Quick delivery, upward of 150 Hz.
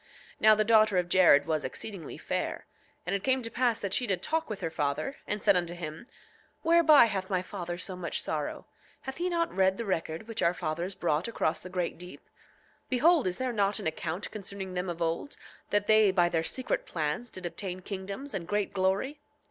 Yes: fast, 210 wpm; high, 190 Hz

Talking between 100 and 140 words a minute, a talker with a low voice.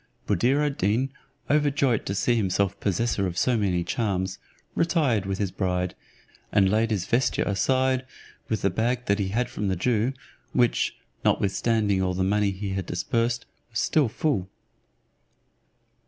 No: average, 155 wpm; low, 105 Hz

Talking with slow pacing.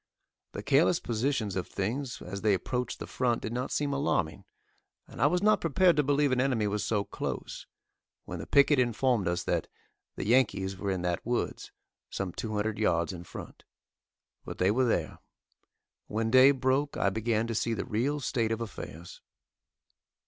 No: average, 180 wpm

